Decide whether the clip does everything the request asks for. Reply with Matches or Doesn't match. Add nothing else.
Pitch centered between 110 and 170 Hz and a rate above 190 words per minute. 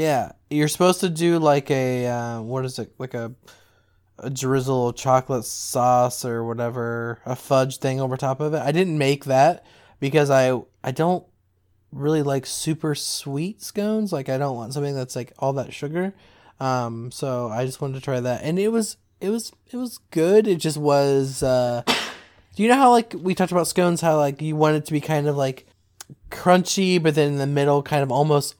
Matches